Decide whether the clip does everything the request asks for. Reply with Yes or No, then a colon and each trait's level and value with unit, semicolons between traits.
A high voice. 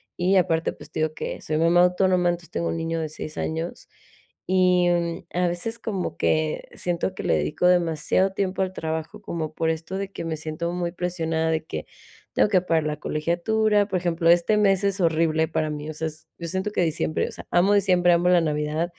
No: medium, 170 Hz